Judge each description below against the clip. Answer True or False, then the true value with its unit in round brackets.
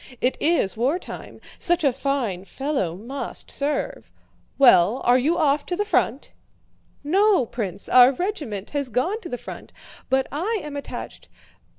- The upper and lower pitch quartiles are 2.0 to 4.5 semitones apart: False (5.1 semitones)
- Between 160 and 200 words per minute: False (150 wpm)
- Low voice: False (275 Hz)